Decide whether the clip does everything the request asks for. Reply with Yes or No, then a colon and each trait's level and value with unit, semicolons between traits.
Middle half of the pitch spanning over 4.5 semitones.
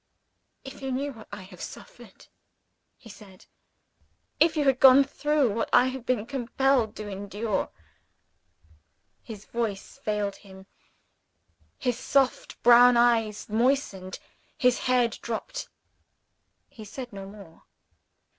No: average, 4.2 semitones